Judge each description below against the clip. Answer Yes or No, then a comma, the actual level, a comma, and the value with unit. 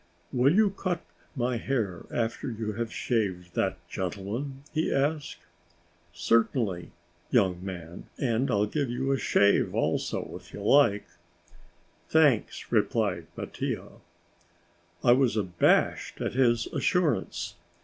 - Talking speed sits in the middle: No, slow, 120 wpm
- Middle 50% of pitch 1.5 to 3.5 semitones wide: No, wide, 5.4 semitones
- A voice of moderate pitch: No, low, 115 Hz